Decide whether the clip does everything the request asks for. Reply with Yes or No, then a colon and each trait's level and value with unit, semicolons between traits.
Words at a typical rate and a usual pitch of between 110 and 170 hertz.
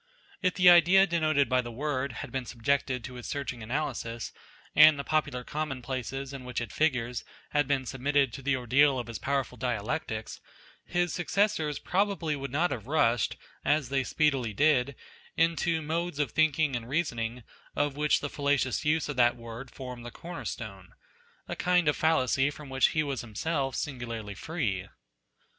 Yes: average, 175 wpm; medium, 140 Hz